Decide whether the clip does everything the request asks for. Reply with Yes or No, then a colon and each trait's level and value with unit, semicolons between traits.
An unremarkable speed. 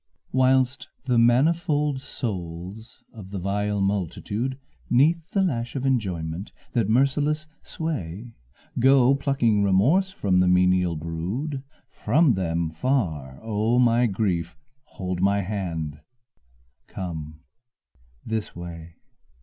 No: slow, 110 wpm